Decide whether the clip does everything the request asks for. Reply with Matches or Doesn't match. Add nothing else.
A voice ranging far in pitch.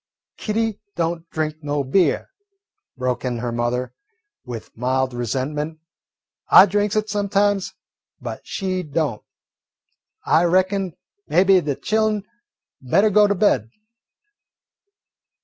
Matches